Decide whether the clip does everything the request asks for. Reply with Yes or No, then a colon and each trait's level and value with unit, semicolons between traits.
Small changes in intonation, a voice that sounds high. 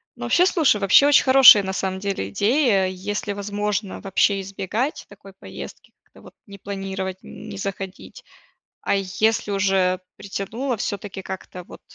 Yes: narrow, 1.6 semitones; high, 200 Hz